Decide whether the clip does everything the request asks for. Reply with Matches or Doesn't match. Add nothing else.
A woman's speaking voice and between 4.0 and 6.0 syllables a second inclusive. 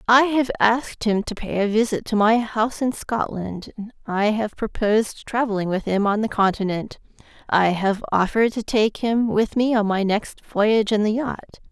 Matches